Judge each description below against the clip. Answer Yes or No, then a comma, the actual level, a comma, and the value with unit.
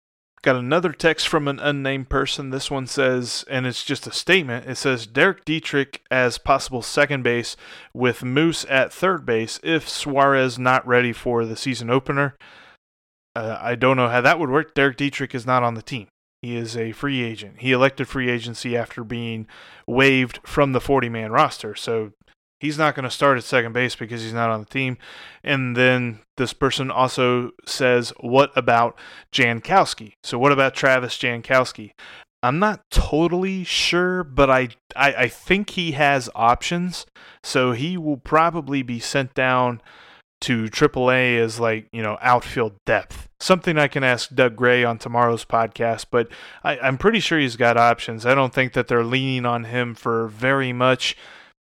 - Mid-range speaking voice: No, low, 130 Hz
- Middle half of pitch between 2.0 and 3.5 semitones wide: Yes, average, 2.8 semitones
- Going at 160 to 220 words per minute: Yes, average, 175 wpm